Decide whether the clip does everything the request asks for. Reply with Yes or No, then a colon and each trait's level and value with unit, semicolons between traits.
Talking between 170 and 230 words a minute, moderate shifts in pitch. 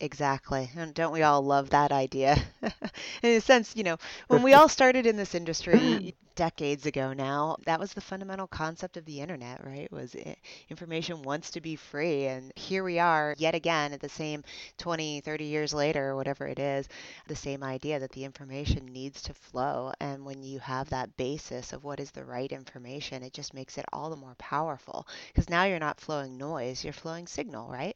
Yes: average, 200 wpm; average, 3.4 semitones